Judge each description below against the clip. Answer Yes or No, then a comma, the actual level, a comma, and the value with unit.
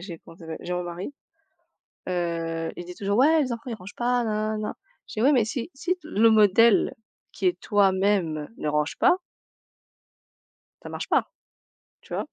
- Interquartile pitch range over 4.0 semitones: Yes, average, 5.1 semitones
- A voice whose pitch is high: Yes, high, 205 Hz